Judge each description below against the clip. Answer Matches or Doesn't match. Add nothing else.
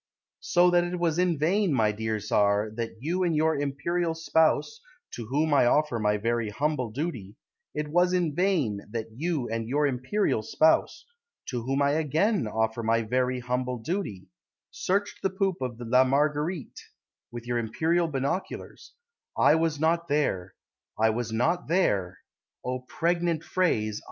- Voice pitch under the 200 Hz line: Matches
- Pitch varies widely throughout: Matches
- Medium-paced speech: Matches